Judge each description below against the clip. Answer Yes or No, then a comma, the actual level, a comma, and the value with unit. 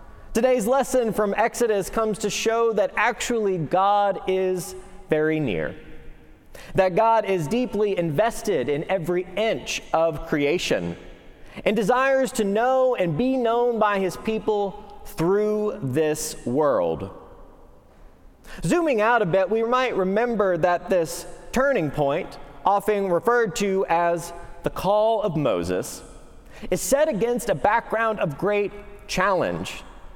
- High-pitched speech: Yes, high, 205 Hz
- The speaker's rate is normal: No, slow, 125 wpm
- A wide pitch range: No, average, 4.4 semitones